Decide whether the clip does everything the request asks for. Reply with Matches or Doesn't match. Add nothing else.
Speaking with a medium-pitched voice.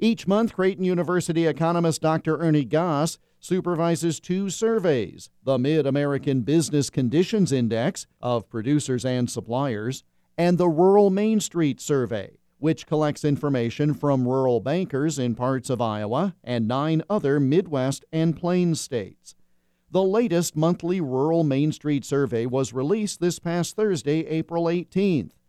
Matches